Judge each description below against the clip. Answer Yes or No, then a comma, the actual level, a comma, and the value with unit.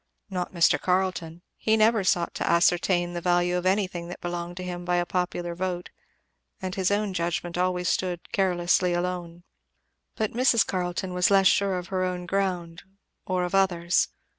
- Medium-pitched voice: Yes, medium, 180 Hz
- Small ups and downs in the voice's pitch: Yes, narrow, 1.3 semitones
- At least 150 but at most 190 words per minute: Yes, average, 170 wpm